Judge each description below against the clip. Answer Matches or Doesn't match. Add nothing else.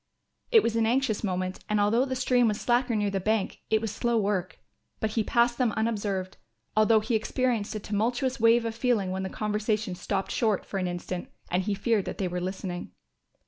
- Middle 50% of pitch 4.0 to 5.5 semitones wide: Doesn't match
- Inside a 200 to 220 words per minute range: Matches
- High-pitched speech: Matches